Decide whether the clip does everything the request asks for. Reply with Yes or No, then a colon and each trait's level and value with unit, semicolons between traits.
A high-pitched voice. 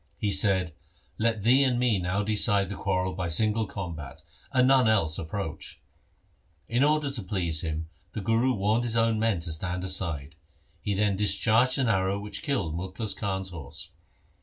No: low, 100 Hz